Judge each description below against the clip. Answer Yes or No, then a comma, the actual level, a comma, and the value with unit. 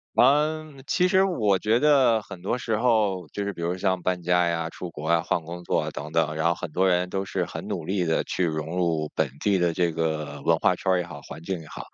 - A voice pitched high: No, very low, 90 Hz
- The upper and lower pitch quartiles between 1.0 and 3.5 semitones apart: No, average, 3.9 semitones